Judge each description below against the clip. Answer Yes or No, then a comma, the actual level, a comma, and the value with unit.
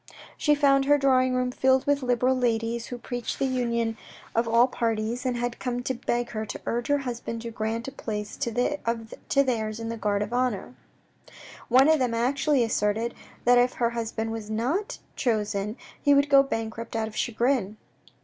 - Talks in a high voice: Yes, high, 240 Hz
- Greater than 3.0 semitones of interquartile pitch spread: No, narrow, 2.4 semitones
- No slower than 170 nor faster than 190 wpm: Yes, average, 185 wpm